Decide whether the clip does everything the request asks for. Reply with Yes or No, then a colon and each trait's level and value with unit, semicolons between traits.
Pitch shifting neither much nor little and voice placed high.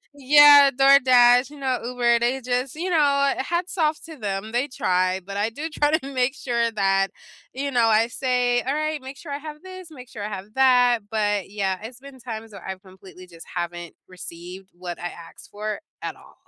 No: wide, 5.7 semitones; high, 245 Hz